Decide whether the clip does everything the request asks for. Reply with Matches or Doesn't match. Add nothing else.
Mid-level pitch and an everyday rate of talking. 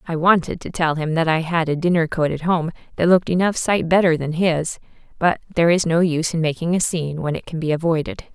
Doesn't match